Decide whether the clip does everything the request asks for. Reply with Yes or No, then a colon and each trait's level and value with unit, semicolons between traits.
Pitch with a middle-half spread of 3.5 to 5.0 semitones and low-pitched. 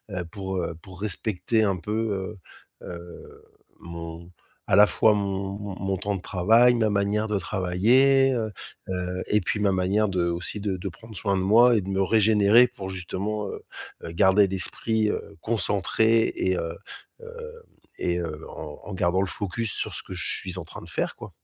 No: average, 2.9 semitones; low, 100 Hz